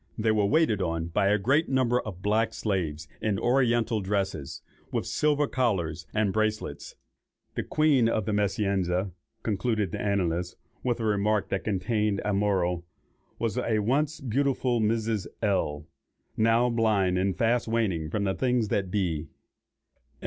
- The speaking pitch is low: Yes, low, 105 Hz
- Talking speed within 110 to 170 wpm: Yes, average, 150 wpm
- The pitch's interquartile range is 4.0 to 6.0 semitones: No, average, 3.4 semitones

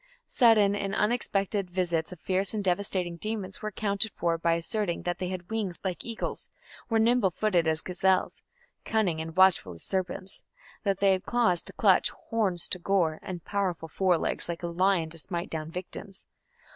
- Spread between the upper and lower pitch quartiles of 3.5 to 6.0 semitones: No, average, 2.8 semitones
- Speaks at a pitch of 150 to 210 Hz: Yes, medium, 185 Hz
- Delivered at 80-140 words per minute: No, average, 180 wpm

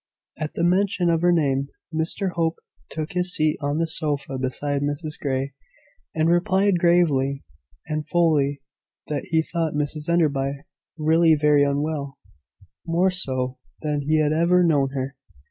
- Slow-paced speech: No, average, 145 wpm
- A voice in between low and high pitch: Yes, medium, 155 Hz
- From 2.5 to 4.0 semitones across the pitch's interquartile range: Yes, average, 3.1 semitones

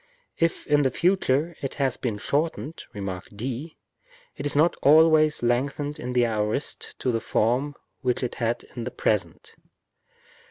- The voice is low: Yes, low, 130 Hz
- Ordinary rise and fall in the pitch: Yes, average, 4.0 semitones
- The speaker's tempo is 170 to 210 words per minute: No, average, 150 wpm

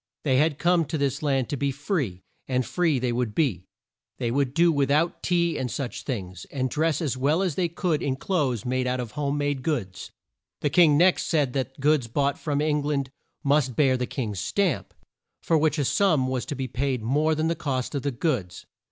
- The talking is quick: Yes, fast, 215 wpm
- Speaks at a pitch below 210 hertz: Yes, medium, 140 Hz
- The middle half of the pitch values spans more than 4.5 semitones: No, average, 3.4 semitones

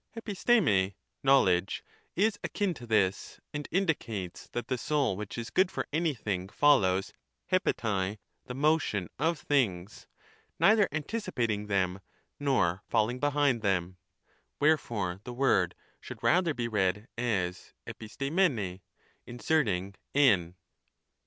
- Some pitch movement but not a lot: No, wide, 7.3 semitones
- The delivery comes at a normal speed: No, slow, 115 wpm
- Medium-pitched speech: No, low, 115 Hz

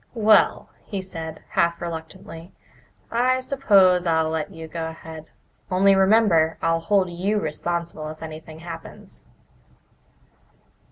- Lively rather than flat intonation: No, average, 3.3 semitones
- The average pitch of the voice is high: No, medium, 170 Hz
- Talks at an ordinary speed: No, slow, 115 wpm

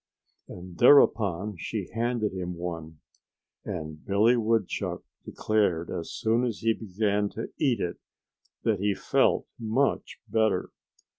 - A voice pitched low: Yes, low, 105 Hz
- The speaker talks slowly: Yes, slow, 125 wpm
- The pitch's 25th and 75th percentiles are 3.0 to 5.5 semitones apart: Yes, average, 4.2 semitones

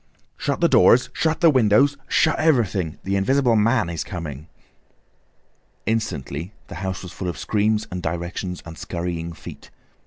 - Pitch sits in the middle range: No, very low, 95 Hz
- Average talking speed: Yes, average, 145 wpm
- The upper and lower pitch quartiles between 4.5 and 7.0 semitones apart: Yes, wide, 5.4 semitones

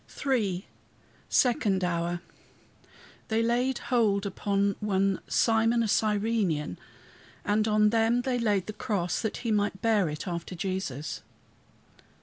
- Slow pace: Yes, slow, 125 wpm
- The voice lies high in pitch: Yes, high, 210 Hz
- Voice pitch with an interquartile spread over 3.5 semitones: No, average, 3.2 semitones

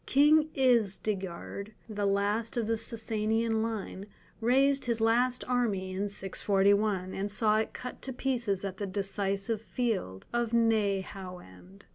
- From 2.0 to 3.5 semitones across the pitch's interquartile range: Yes, average, 3.0 semitones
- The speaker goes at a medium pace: No, slow, 130 wpm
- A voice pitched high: Yes, high, 215 Hz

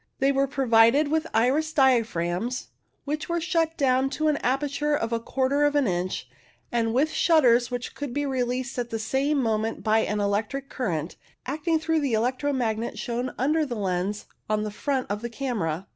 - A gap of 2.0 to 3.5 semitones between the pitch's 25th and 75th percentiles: No, average, 4.3 semitones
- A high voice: Yes, very high, 255 Hz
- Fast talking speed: No, average, 190 wpm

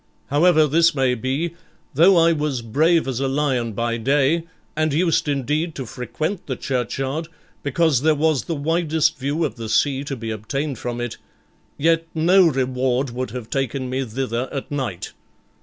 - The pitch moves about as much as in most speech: Yes, average, 3.9 semitones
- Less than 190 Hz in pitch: Yes, medium, 140 Hz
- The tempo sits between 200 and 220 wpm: No, average, 170 wpm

